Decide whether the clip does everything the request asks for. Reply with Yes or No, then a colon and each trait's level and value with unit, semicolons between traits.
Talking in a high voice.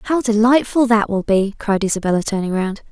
Yes: high, 215 Hz